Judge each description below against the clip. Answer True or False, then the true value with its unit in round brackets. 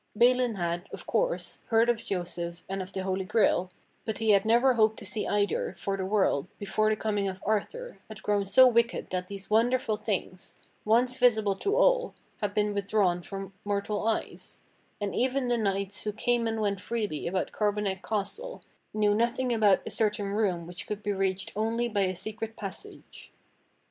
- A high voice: True (210 Hz)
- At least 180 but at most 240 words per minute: True (185 wpm)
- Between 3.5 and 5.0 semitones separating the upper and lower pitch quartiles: False (2.8 semitones)